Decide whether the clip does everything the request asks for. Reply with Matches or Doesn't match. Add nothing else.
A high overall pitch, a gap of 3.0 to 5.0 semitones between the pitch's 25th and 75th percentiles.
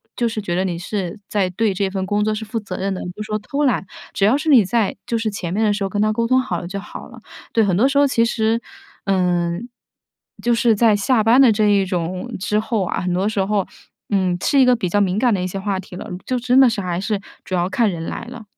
Matches